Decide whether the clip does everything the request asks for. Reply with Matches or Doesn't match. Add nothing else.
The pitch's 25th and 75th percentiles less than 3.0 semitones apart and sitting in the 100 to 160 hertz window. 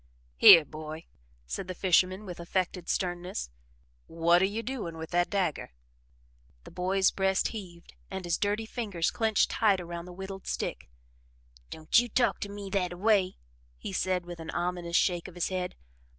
Doesn't match